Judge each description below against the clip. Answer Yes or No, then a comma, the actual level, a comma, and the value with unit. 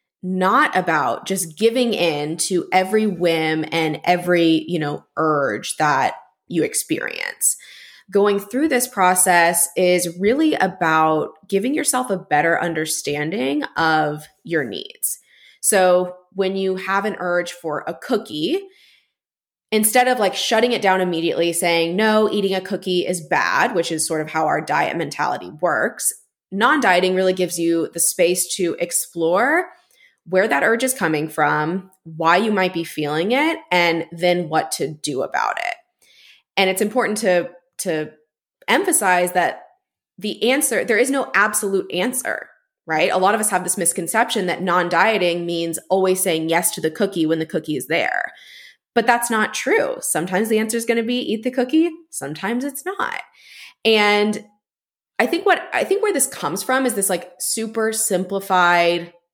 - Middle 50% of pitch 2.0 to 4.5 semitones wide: No, average, 5.0 semitones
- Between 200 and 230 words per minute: No, average, 160 wpm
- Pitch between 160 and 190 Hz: Yes, medium, 185 Hz